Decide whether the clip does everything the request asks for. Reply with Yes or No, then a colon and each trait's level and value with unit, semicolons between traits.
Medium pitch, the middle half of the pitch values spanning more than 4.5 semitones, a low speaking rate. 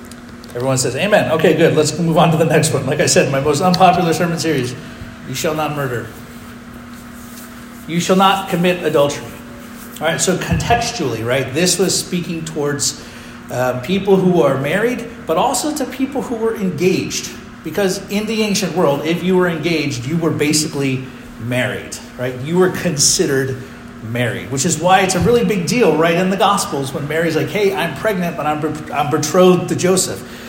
No: medium, 165 Hz; average, 5.2 semitones; average, 180 wpm